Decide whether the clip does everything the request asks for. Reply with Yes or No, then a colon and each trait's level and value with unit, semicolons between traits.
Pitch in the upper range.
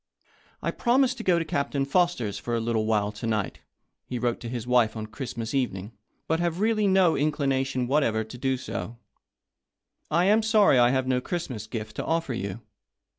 No: low, 130 Hz